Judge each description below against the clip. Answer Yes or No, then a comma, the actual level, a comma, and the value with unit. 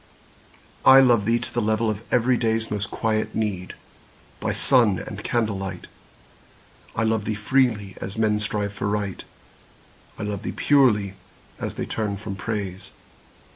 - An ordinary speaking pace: Yes, average, 145 wpm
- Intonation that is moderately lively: No, narrow, 2.0 semitones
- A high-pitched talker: No, low, 105 Hz